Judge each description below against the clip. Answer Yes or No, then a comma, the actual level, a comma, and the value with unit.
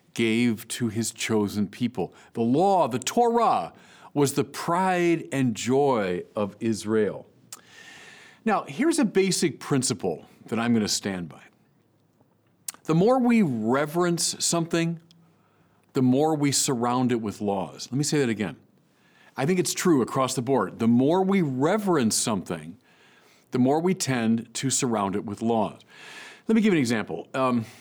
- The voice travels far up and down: Yes, wide, 7.3 semitones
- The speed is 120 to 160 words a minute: Yes, average, 155 wpm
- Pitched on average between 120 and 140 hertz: Yes, low, 135 Hz